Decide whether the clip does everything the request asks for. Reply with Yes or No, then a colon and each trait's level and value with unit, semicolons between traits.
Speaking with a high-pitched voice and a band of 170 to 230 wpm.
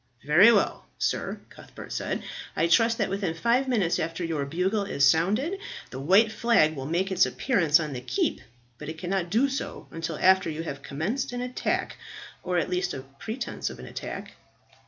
No: medium, 180 Hz; average, 185 wpm